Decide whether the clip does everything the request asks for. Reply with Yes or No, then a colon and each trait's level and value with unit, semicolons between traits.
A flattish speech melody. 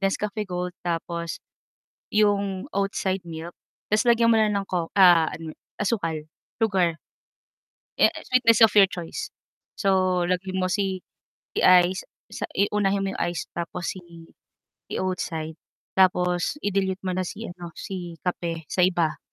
Yes: narrow, 2.3 semitones